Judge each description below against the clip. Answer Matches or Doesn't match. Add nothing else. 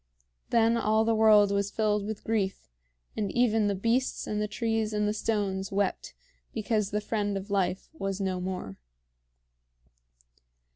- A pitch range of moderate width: Doesn't match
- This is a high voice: Matches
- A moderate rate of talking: Matches